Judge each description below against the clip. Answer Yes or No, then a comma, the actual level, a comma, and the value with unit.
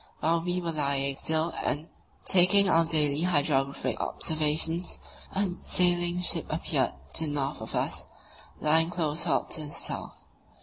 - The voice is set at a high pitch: No, medium, 160 Hz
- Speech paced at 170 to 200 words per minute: No, average, 145 wpm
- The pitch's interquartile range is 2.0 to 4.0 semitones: Yes, average, 2.8 semitones